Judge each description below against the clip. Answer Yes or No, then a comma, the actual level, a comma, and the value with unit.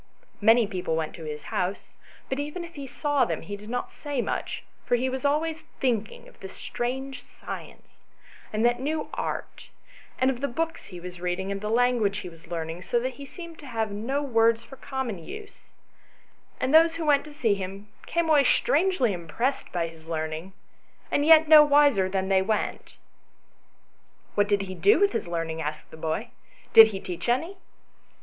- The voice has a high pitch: Yes, high, 235 Hz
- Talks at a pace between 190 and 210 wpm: Yes, average, 195 wpm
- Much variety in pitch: Yes, wide, 7.3 semitones